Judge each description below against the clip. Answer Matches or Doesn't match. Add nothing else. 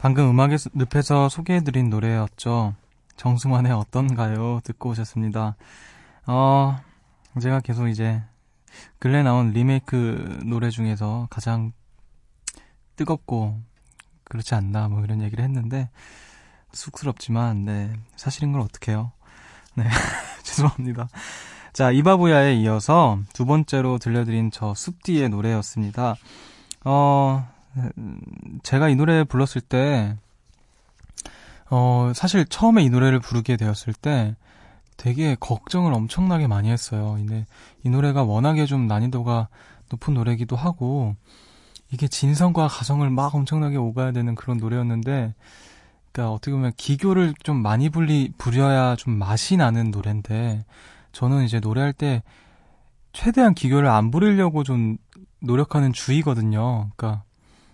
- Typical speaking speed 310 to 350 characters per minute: Doesn't match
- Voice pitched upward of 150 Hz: Doesn't match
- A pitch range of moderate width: Matches